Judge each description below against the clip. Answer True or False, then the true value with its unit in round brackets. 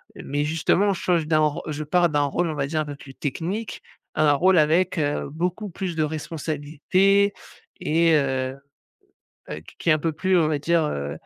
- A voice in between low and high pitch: True (155 Hz)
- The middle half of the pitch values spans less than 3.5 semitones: True (3.1 semitones)